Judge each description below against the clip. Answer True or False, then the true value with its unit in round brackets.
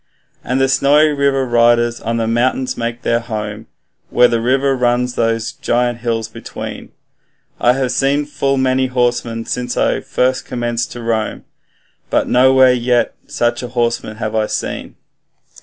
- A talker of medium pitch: False (120 Hz)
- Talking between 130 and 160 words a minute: True (150 wpm)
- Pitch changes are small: True (1.9 semitones)